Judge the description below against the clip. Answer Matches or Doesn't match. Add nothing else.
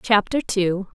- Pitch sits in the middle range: Doesn't match